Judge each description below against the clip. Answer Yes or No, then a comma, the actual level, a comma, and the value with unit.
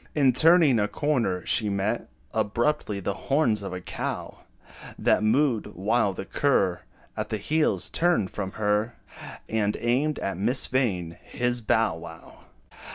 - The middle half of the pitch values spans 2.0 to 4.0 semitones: No, average, 5.0 semitones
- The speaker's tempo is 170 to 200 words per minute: No, average, 145 wpm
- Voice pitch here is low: Yes, low, 110 Hz